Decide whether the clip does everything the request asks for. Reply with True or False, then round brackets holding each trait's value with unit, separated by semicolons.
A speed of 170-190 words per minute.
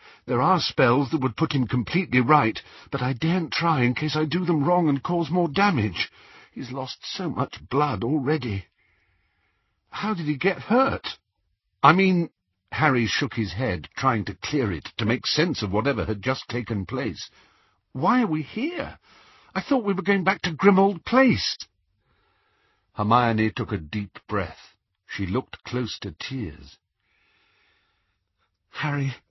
False (160 wpm)